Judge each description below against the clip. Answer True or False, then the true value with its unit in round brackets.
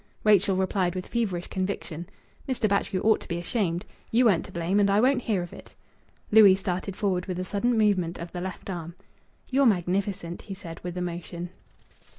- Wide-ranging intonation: False (2.8 semitones)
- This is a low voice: False (185 Hz)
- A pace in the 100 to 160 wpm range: False (185 wpm)